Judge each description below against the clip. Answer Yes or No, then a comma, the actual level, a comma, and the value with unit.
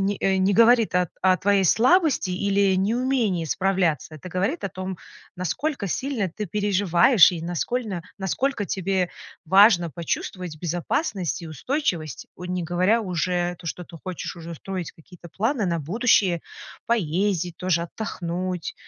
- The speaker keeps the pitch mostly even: No, average, 3.0 semitones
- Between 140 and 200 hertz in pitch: Yes, medium, 185 Hz